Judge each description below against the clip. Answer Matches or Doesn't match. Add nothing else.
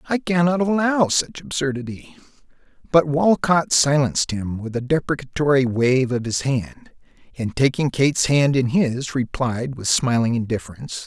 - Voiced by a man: Matches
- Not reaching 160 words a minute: Matches